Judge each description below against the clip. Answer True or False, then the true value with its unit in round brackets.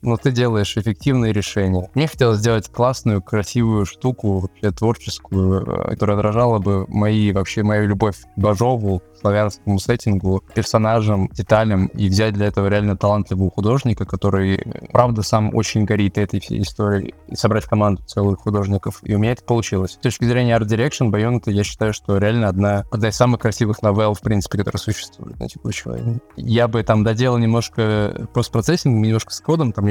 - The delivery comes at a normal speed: False (170 wpm)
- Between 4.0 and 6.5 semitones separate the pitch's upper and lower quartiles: False (2.4 semitones)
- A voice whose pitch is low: True (105 Hz)